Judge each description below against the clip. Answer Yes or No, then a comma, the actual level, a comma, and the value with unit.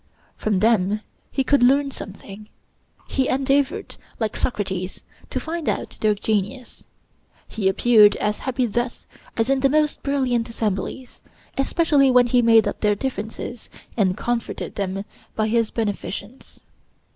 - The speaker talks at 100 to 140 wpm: Yes, slow, 135 wpm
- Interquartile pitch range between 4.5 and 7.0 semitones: No, average, 4.1 semitones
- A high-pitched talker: Yes, high, 230 Hz